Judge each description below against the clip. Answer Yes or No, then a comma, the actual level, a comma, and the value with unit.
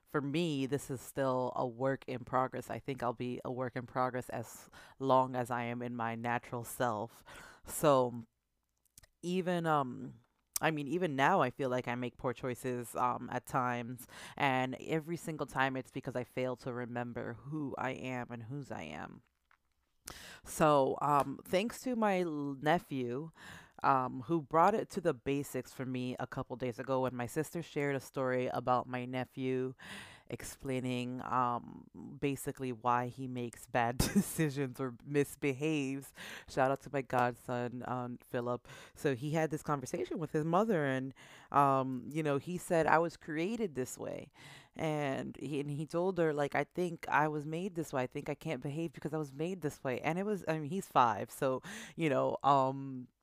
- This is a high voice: No, low, 135 Hz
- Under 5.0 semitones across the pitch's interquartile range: Yes, average, 3.4 semitones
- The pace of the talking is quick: No, average, 180 wpm